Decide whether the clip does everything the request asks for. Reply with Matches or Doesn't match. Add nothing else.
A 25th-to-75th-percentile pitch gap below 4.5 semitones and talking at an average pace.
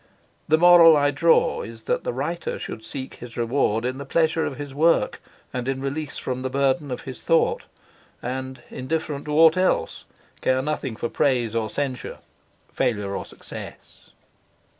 Matches